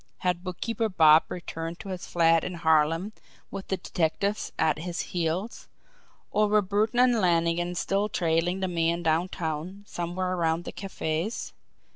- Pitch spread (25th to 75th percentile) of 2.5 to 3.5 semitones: Yes, average, 2.9 semitones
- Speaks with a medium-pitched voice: Yes, medium, 175 Hz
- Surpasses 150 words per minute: No, average, 145 wpm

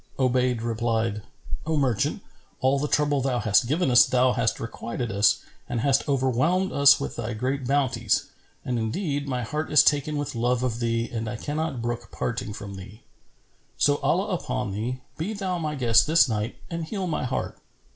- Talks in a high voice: No, low, 130 Hz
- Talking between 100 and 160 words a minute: No, average, 180 wpm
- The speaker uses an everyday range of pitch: Yes, average, 4.0 semitones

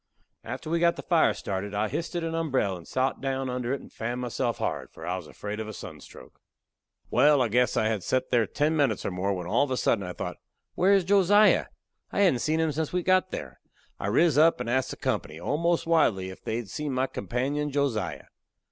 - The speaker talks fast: Yes, fast, 230 wpm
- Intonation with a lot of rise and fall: Yes, wide, 7.1 semitones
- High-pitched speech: No, low, 130 Hz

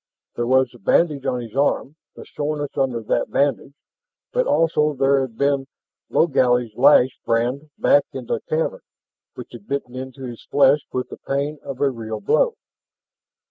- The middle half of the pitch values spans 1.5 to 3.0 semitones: Yes, average, 2.7 semitones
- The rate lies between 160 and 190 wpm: Yes, average, 165 wpm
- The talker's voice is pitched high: No, low, 135 Hz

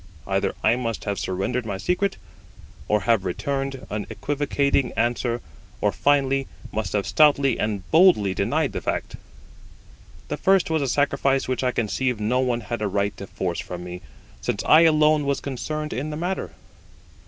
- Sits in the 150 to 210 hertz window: No, low, 125 Hz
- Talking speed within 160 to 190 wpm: Yes, average, 165 wpm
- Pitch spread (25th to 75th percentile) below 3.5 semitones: No, wide, 5.4 semitones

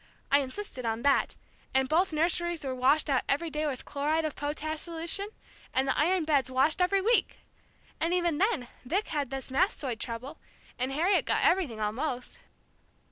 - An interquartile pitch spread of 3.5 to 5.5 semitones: Yes, average, 4.6 semitones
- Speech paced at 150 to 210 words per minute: Yes, average, 170 wpm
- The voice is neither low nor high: No, very high, 300 Hz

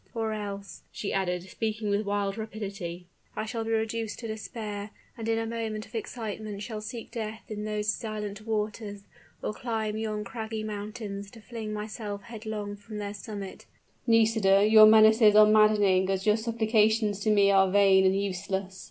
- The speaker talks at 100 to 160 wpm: No, average, 170 wpm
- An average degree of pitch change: No, narrow, 1.5 semitones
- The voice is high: Yes, high, 215 Hz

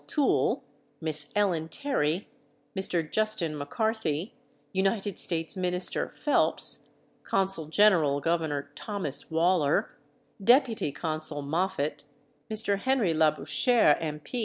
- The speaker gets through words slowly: Yes, slow, 95 wpm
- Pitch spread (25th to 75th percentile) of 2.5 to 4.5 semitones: No, average, 5.1 semitones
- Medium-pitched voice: Yes, medium, 170 Hz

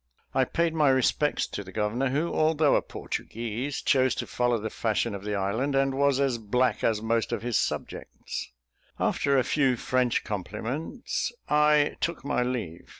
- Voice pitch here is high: No, low, 130 Hz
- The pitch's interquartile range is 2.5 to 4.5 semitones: Yes, average, 4.2 semitones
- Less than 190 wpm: Yes, average, 170 wpm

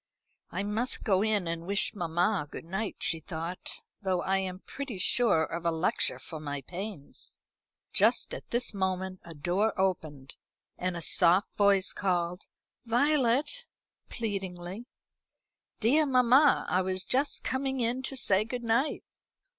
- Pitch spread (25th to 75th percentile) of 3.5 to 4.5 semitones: No, average, 5.1 semitones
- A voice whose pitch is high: Yes, high, 195 Hz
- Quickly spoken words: No, average, 145 wpm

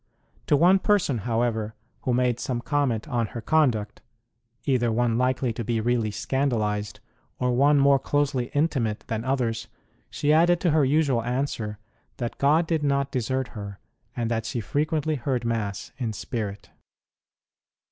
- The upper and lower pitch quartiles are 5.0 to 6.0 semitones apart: No, average, 4.0 semitones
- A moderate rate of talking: Yes, average, 150 wpm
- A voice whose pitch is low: Yes, low, 125 Hz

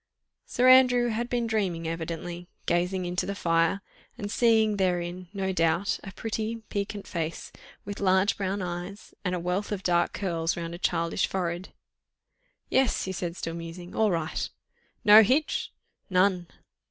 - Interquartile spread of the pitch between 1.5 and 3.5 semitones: Yes, average, 3.2 semitones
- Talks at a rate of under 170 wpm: Yes, average, 155 wpm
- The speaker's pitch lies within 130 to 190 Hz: Yes, medium, 185 Hz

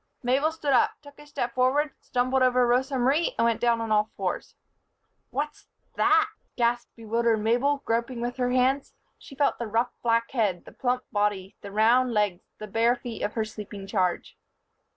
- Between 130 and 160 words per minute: No, average, 180 wpm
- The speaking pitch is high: Yes, high, 240 Hz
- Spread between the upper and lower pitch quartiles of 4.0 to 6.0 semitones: No, average, 3.0 semitones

